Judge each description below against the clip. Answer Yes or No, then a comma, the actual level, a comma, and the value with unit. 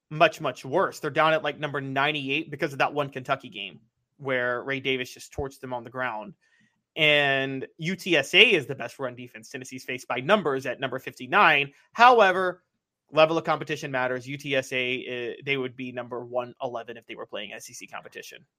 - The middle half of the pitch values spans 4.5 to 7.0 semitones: No, average, 3.5 semitones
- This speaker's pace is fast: No, average, 180 wpm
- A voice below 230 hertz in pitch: Yes, low, 135 Hz